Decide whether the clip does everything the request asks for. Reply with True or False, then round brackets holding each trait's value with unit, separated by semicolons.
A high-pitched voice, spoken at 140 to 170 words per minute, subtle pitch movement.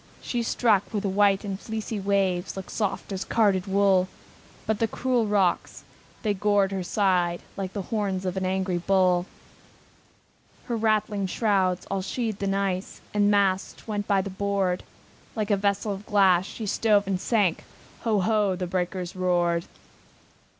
True (195 Hz; 165 wpm; 1.9 semitones)